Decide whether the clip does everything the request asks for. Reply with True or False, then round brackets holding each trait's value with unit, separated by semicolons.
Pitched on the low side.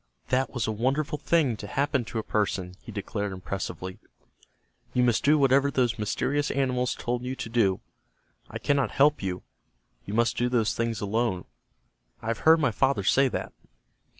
True (120 Hz)